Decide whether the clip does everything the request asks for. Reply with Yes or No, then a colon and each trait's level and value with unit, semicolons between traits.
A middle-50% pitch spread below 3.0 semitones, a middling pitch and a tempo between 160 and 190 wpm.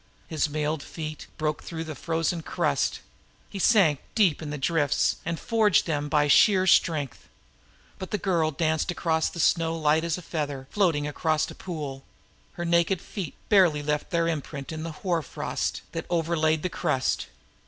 Yes: narrow, 2.4 semitones; medium, 160 Hz; average, 165 wpm